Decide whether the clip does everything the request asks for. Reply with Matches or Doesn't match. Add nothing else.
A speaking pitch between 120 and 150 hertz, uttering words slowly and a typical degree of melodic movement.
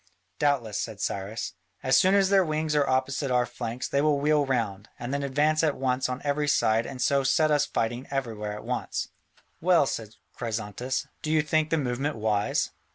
Doesn't match